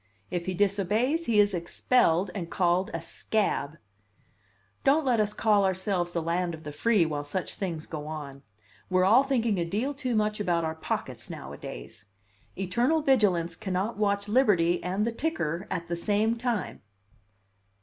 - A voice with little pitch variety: No, average, 4.6 semitones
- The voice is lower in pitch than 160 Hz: No, high, 190 Hz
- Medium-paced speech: Yes, average, 160 wpm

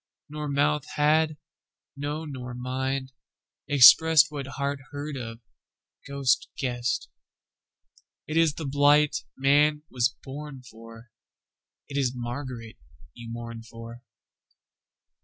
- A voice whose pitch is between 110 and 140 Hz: Yes, low, 135 Hz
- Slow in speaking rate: Yes, slow, 95 wpm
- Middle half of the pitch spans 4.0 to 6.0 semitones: No, average, 3.3 semitones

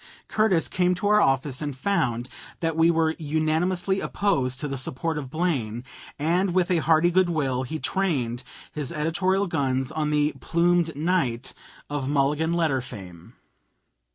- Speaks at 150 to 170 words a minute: Yes, average, 155 wpm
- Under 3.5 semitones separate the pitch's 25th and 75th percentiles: No, average, 4.6 semitones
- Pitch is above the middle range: No, medium, 155 Hz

